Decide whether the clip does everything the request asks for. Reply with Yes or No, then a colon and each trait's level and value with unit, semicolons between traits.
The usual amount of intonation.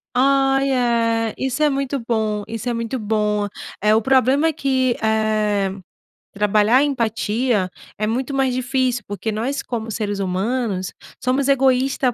Yes: average, 3.7 semitones